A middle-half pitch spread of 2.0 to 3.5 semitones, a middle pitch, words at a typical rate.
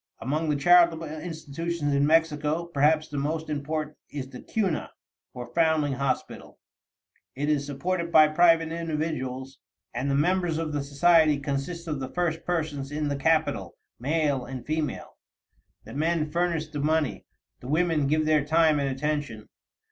Yes: narrow, 2.5 semitones; medium, 155 Hz; average, 155 wpm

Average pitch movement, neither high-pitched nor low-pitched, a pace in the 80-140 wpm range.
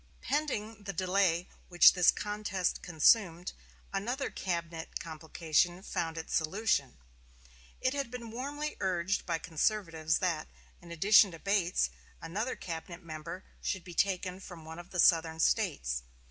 Yes: average, 3.8 semitones; medium, 180 Hz; slow, 135 wpm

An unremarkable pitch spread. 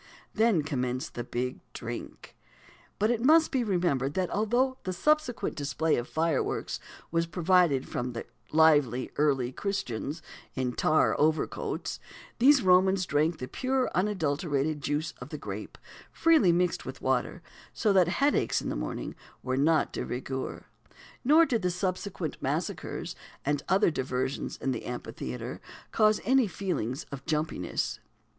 No: wide, 6.7 semitones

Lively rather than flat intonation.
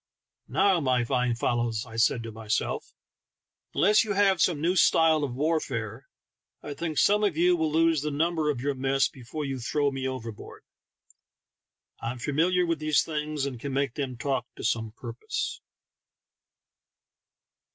No: average, 4.8 semitones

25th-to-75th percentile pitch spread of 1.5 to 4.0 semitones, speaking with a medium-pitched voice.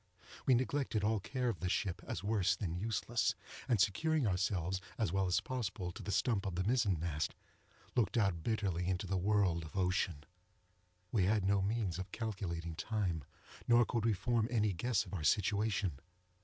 No: average, 3.5 semitones; low, 100 Hz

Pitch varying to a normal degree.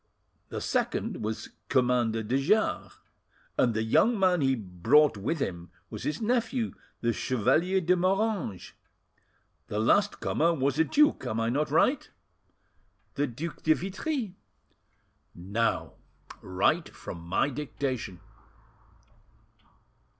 No: wide, 8.6 semitones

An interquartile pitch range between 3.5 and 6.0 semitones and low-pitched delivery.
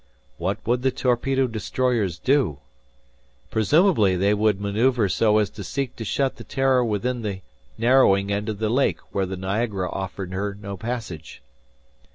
Yes: average, 4.1 semitones; low, 110 Hz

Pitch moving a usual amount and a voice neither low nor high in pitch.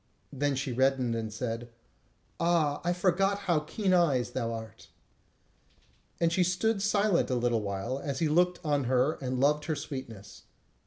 No: wide, 5.9 semitones; medium, 145 Hz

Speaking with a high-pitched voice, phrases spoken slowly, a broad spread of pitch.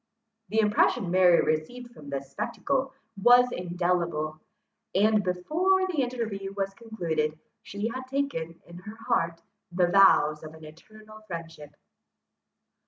Yes: high, 195 Hz; slow, 125 wpm; wide, 6.0 semitones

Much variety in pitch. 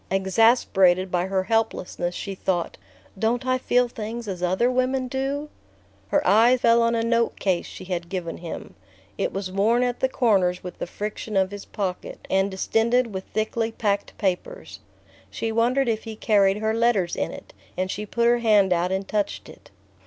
No: average, 3.7 semitones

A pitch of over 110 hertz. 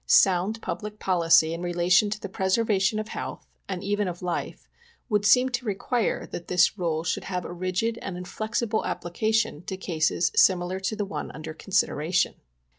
Yes: high, 190 Hz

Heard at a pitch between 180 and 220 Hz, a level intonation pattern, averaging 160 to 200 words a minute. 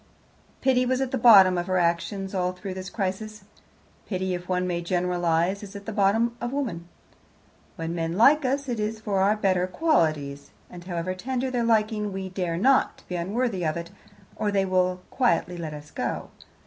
No: high, 190 Hz; average, 3.9 semitones; average, 185 wpm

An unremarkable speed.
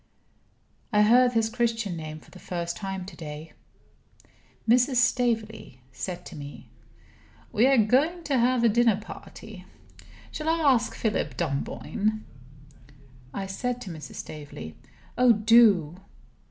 No: slow, 130 wpm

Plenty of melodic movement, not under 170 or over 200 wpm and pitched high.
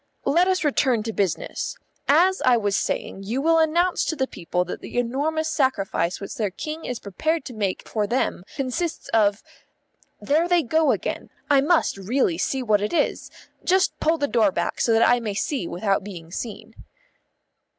Yes: wide, 7.6 semitones; average, 180 wpm; high, 245 Hz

